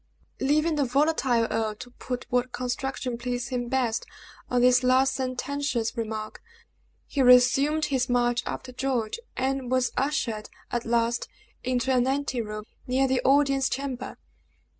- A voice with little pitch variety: Yes, narrow, 1.8 semitones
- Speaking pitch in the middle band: No, very high, 255 Hz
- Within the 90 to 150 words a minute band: Yes, average, 140 wpm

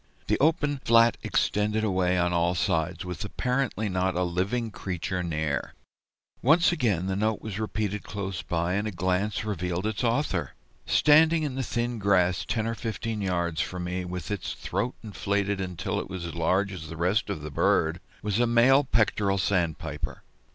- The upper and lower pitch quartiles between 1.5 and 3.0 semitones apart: No, average, 4.0 semitones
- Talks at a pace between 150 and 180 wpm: Yes, average, 175 wpm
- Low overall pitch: Yes, low, 100 Hz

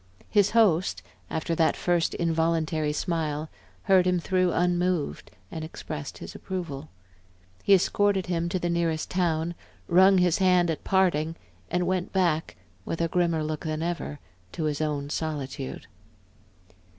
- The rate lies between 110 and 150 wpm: Yes, average, 140 wpm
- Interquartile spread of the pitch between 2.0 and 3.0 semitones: Yes, narrow, 2.5 semitones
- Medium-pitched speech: Yes, medium, 170 Hz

